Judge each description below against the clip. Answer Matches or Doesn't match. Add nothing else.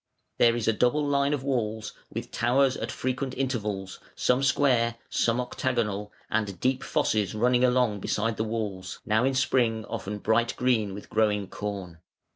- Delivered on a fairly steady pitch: Doesn't match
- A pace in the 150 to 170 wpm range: Matches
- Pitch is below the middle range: Matches